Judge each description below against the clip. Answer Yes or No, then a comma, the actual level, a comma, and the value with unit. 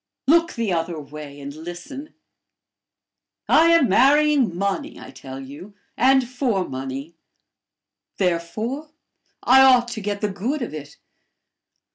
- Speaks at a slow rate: Yes, slow, 125 wpm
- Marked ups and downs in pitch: Yes, wide, 8.4 semitones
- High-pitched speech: Yes, high, 205 Hz